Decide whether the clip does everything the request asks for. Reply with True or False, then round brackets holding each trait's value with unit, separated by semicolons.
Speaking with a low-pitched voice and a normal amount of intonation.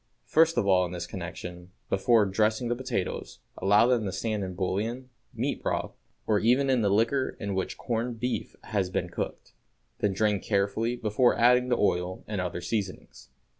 True (105 Hz; 4.1 semitones)